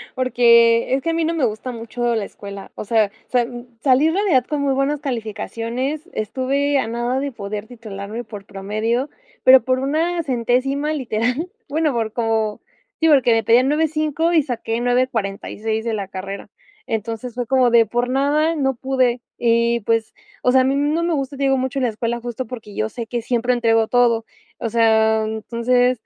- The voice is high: Yes, high, 245 Hz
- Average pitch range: Yes, average, 3.2 semitones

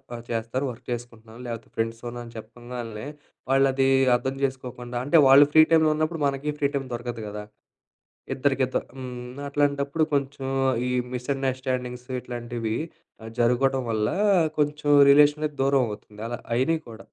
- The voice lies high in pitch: No, low, 130 Hz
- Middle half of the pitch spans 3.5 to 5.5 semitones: No, average, 2.7 semitones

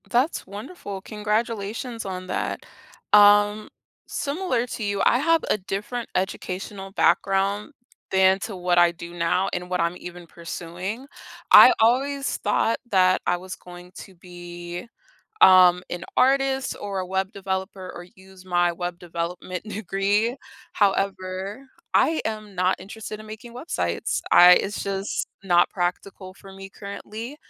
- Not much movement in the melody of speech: No, average, 3.0 semitones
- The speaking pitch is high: Yes, high, 195 Hz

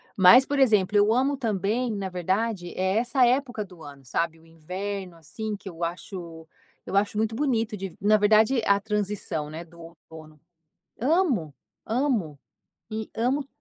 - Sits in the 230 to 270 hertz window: No, high, 205 Hz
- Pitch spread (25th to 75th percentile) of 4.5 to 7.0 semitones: Yes, average, 5.0 semitones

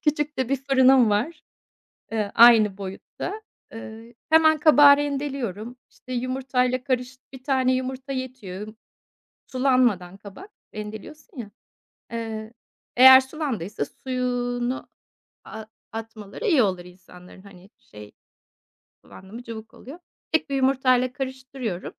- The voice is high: Yes, very high, 250 Hz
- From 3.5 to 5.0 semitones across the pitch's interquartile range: Yes, average, 3.8 semitones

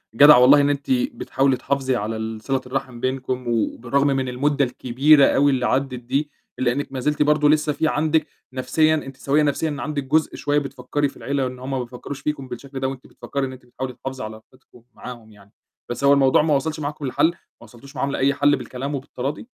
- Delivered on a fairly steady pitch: Yes, narrow, 2.3 semitones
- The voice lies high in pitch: No, low, 135 Hz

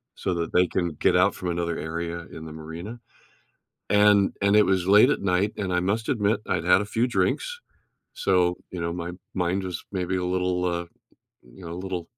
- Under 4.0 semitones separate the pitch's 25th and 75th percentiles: Yes, average, 2.7 semitones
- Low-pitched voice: Yes, very low, 90 Hz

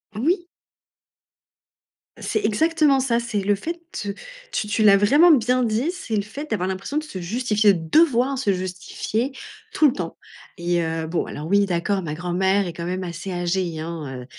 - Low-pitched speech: No, high, 200 Hz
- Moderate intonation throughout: No, wide, 6.3 semitones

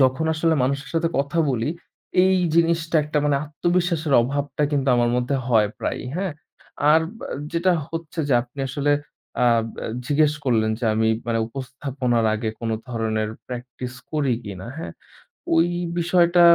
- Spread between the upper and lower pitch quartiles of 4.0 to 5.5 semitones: Yes, average, 5.2 semitones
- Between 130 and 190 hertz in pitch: Yes, medium, 140 Hz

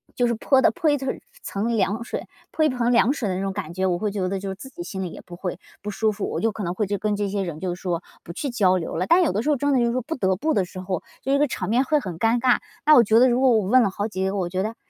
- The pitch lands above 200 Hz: Yes, high, 210 Hz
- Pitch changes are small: No, average, 5.1 semitones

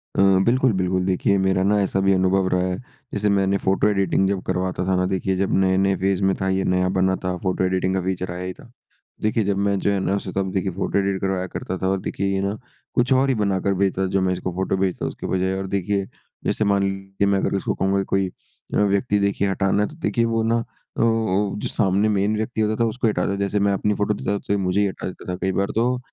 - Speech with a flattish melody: Yes, narrow, 1.3 semitones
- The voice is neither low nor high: No, very low, 95 Hz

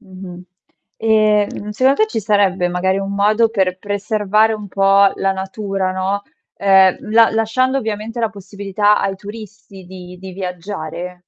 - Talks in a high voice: Yes, high, 200 Hz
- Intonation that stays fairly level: Yes, narrow, 2.3 semitones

